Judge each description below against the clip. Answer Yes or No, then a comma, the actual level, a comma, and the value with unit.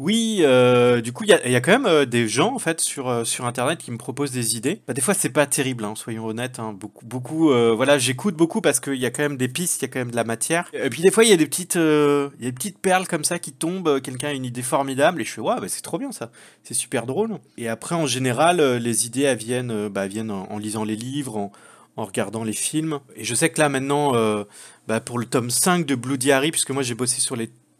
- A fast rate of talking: Yes, fast, 280 wpm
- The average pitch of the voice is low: Yes, low, 130 Hz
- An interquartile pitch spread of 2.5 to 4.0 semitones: No, average, 4.4 semitones